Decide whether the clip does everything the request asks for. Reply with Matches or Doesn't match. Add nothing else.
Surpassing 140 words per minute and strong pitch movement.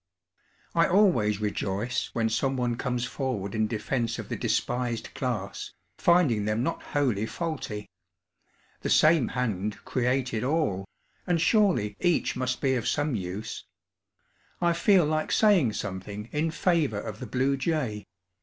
Doesn't match